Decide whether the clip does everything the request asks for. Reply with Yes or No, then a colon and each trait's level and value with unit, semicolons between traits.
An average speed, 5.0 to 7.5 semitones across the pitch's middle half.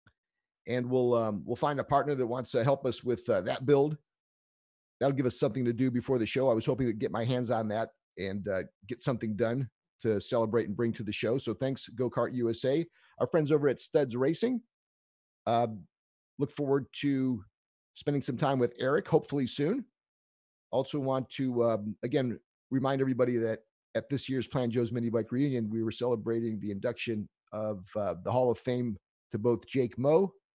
No: average, 195 wpm; average, 3.2 semitones